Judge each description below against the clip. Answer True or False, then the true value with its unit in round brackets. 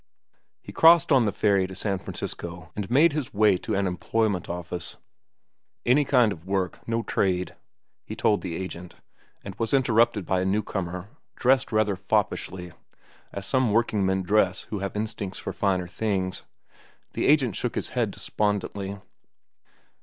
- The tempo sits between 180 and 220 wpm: False (155 wpm)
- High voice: False (100 Hz)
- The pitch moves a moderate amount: True (3.5 semitones)